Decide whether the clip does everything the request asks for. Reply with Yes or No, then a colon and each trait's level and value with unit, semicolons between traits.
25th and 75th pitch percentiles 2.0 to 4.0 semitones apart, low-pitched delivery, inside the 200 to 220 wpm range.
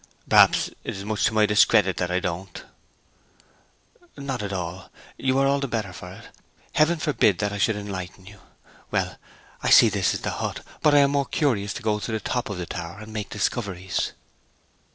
No: average, 4.6 semitones; low, 105 Hz; fast, 205 wpm